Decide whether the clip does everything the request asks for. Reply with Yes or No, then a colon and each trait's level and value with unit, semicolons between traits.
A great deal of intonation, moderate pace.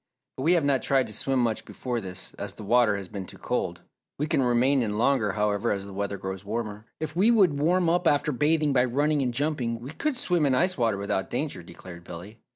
No: wide, 6.1 semitones; fast, 235 wpm